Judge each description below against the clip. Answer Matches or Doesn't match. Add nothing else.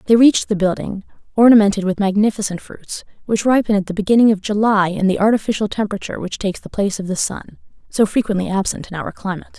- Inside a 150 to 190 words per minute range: Doesn't match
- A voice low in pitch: Doesn't match